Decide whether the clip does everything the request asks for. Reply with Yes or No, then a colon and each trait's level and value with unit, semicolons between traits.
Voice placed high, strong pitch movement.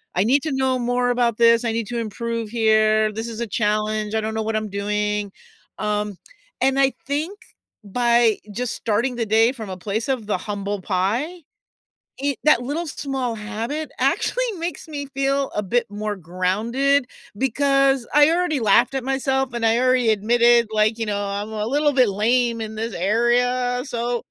No: high, 235 Hz; average, 3.8 semitones